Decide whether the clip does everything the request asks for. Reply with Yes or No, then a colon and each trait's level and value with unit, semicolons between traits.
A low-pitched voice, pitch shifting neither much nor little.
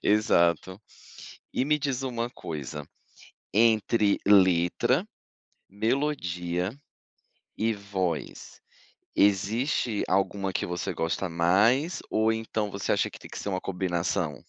Yes: low, 100 Hz; average, 4.1 semitones